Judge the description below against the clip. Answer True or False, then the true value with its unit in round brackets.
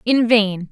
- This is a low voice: False (215 Hz)